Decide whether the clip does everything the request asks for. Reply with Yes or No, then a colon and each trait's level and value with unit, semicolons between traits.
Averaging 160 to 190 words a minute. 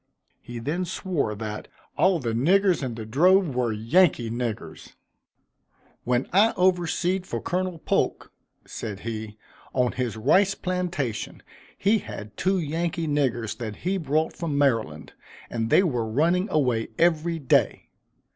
No: slow, 135 wpm